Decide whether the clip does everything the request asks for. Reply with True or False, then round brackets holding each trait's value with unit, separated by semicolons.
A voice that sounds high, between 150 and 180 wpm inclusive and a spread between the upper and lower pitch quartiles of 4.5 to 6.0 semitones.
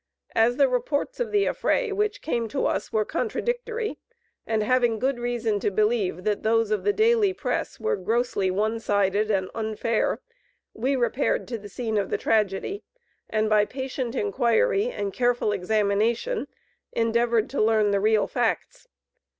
True (230 Hz; 160 wpm; 5.0 semitones)